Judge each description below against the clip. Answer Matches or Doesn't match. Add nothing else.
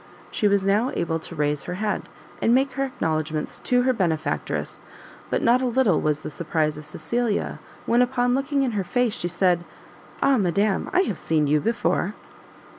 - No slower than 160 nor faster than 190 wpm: Matches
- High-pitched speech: Matches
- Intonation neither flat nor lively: Doesn't match